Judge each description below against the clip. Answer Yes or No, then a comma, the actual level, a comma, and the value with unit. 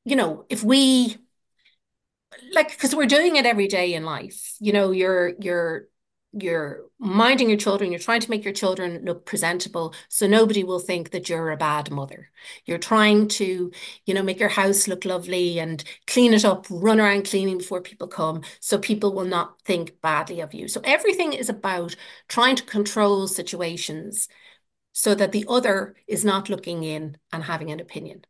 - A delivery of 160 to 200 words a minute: Yes, average, 180 wpm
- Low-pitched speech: No, high, 195 Hz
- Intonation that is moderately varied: Yes, average, 3.8 semitones